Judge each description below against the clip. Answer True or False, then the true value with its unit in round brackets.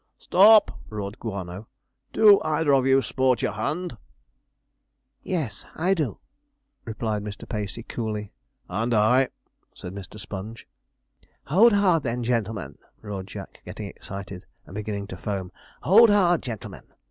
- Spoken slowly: True (130 wpm)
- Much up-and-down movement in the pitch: True (7.4 semitones)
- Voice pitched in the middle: False (115 Hz)